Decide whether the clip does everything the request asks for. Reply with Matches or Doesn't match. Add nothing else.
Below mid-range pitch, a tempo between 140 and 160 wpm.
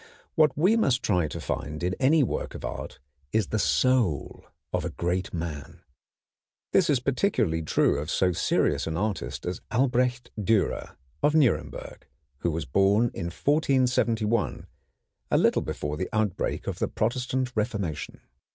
Matches